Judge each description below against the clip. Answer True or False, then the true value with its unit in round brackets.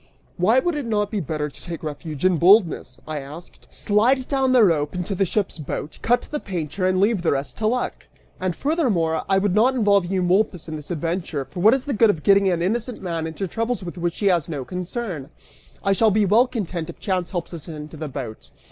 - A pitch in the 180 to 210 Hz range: True (185 Hz)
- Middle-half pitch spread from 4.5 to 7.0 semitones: True (5.0 semitones)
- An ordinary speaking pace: False (225 wpm)